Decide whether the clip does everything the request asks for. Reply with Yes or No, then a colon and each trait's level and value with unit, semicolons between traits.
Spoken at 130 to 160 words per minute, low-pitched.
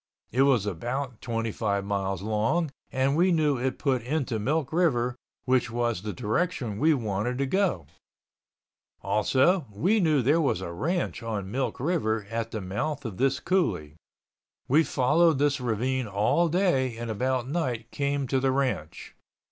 Yes: average, 155 wpm; low, 130 Hz